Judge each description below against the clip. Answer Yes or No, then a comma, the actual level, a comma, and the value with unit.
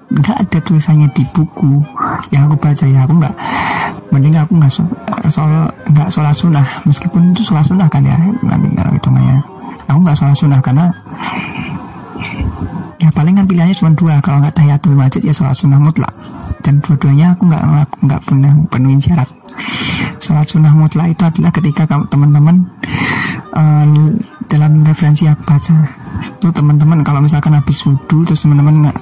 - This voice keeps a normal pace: No, fast, 165 wpm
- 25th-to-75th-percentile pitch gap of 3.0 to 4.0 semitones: No, narrow, 2.4 semitones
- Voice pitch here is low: No, medium, 155 Hz